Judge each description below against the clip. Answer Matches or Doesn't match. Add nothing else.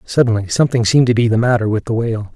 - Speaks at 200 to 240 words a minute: Doesn't match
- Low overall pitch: Matches